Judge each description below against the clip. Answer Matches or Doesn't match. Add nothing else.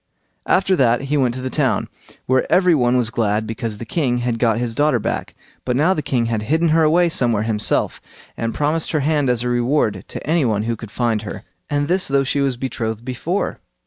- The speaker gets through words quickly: Matches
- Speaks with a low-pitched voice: Matches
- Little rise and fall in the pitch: Doesn't match